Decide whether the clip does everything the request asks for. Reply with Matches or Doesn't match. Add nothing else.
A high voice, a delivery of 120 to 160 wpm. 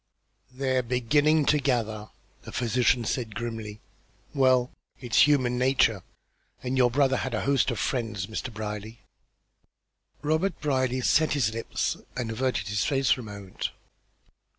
Doesn't match